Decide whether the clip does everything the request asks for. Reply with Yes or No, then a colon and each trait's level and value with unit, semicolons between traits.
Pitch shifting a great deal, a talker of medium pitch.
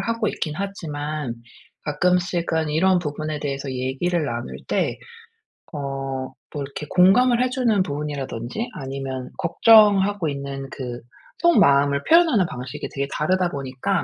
Yes: wide, 5.7 semitones; medium, 155 Hz